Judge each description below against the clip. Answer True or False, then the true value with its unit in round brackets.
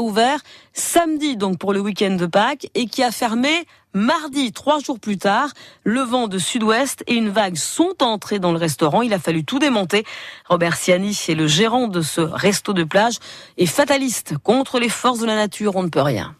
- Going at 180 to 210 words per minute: True (205 wpm)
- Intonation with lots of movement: True (5.8 semitones)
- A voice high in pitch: True (215 Hz)